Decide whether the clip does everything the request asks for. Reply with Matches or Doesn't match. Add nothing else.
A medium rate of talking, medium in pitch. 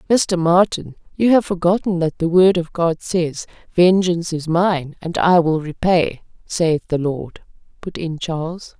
Matches